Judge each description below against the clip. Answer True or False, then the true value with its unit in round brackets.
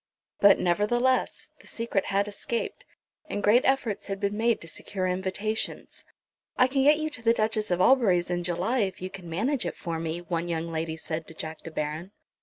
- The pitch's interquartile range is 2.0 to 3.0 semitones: False (5.1 semitones)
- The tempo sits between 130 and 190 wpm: False (200 wpm)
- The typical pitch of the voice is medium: False (195 Hz)